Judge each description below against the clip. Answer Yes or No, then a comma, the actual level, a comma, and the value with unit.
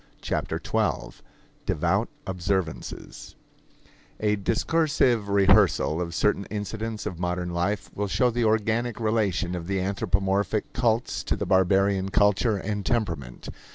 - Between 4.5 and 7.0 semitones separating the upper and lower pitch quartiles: No, average, 2.9 semitones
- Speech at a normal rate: No, slow, 125 wpm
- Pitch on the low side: Yes, low, 100 Hz